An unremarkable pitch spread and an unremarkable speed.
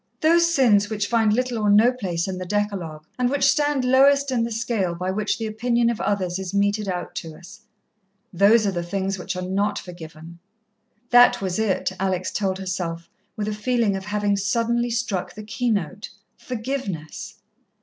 Yes: average, 4.1 semitones; average, 180 wpm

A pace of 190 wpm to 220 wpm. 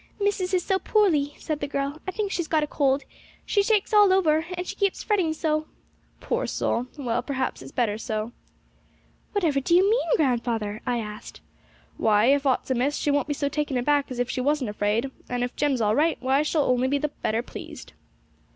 Yes: fast, 205 wpm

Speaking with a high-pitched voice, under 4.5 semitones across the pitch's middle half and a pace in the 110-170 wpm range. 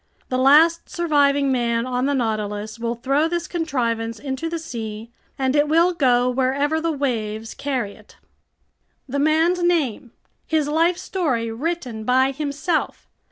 No: very high, 275 Hz; average, 5.1 semitones; average, 145 wpm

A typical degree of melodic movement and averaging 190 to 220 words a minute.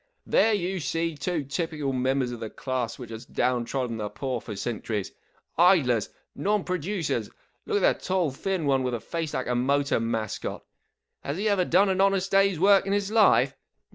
No: wide, 7.4 semitones; average, 200 wpm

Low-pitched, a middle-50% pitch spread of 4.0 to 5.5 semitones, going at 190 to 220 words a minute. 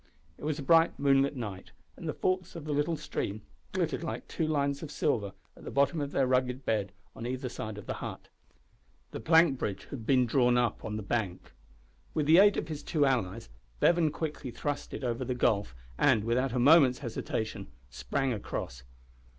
Yes: low, 130 Hz; average, 4.7 semitones; average, 195 wpm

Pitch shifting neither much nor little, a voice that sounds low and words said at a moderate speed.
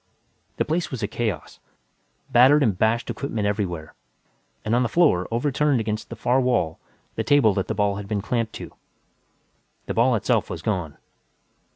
Yes: average, 3.9 semitones; low, 110 Hz; average, 170 wpm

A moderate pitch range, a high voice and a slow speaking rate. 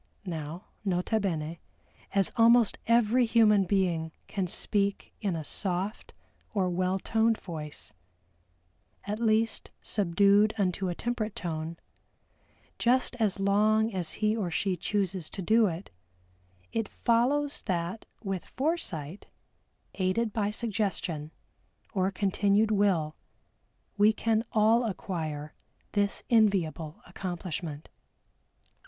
Yes: average, 3.8 semitones; high, 200 Hz; slow, 110 wpm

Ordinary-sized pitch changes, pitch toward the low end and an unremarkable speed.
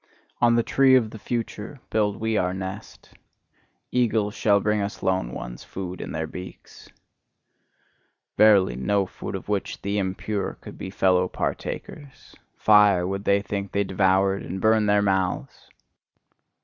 No: narrow, 2.2 semitones; low, 100 Hz; average, 150 wpm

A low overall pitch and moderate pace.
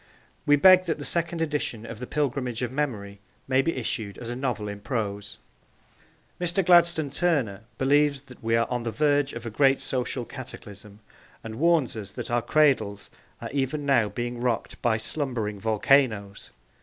Yes: low, 125 Hz; average, 170 wpm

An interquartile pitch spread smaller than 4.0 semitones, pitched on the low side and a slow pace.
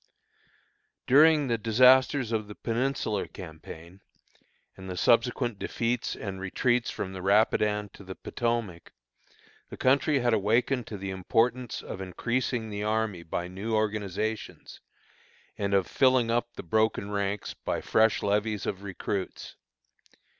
Yes: average, 3.6 semitones; low, 110 Hz; slow, 130 wpm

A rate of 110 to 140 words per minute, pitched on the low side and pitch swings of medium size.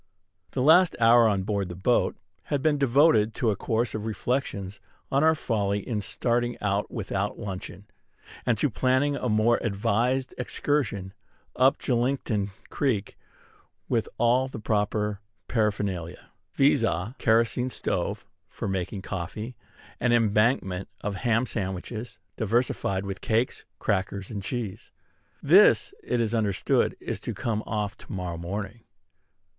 Yes: slow, 135 wpm; low, 110 Hz; average, 3.6 semitones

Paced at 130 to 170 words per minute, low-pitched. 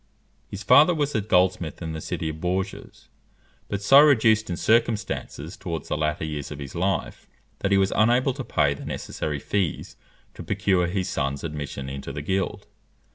No: average, 180 wpm; very low, 90 Hz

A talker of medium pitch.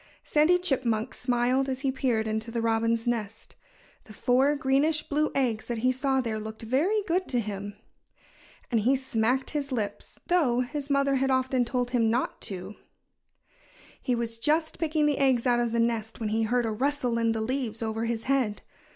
No: high, 245 Hz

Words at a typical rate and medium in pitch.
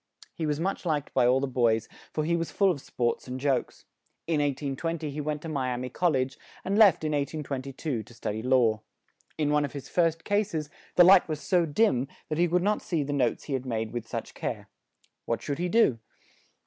No: fast, 225 wpm; medium, 145 Hz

